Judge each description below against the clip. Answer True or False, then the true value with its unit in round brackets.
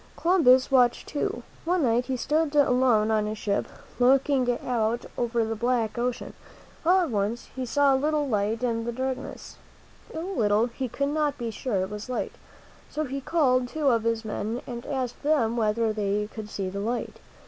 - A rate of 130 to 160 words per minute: False (195 wpm)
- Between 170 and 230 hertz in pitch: False (245 Hz)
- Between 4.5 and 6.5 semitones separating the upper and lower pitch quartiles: False (3.7 semitones)